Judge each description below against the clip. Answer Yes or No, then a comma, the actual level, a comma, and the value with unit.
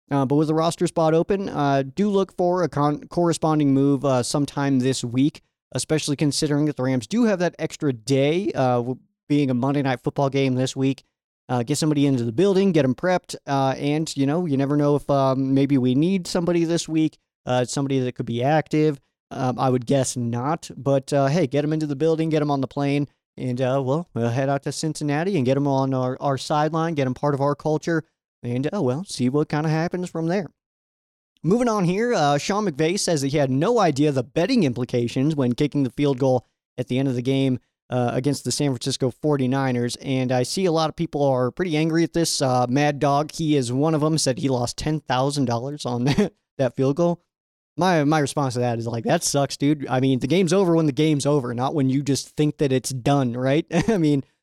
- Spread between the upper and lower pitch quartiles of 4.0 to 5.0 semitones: No, average, 3.1 semitones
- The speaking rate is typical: No, fast, 230 wpm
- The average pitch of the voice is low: No, medium, 145 Hz